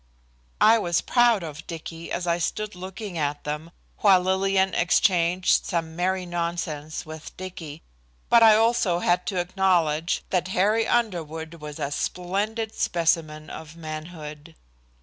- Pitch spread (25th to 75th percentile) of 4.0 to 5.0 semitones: No, average, 3.1 semitones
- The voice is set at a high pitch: No, medium, 175 Hz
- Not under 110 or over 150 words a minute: Yes, slow, 135 wpm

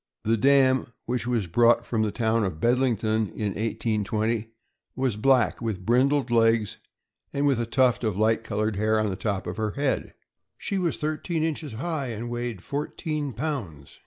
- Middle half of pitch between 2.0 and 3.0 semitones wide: No, average, 3.6 semitones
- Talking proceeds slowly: No, average, 175 wpm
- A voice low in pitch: Yes, low, 115 Hz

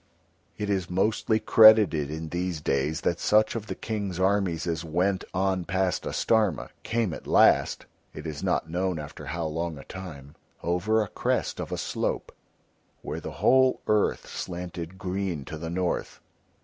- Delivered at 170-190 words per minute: No, average, 160 wpm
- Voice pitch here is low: Yes, very low, 90 Hz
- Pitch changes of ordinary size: Yes, average, 3.6 semitones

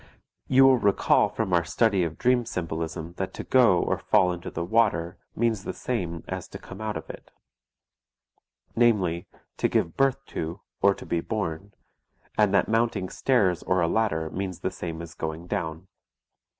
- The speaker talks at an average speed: Yes, average, 175 wpm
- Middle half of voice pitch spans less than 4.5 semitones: No, average, 4.8 semitones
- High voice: No, very low, 95 Hz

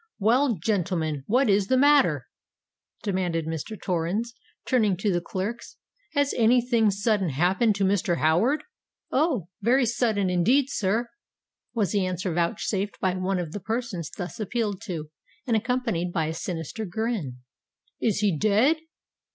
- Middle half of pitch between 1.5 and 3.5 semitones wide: No, average, 4.9 semitones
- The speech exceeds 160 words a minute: No, average, 145 wpm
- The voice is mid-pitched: No, high, 200 Hz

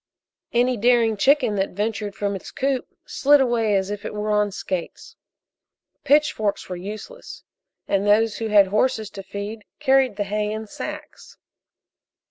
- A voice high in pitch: Yes, high, 215 Hz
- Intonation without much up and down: No, average, 3.2 semitones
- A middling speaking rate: Yes, average, 150 wpm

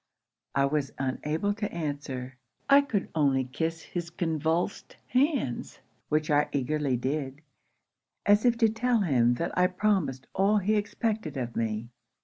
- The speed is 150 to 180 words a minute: No, average, 140 wpm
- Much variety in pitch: Yes, wide, 7.2 semitones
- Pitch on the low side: No, medium, 160 Hz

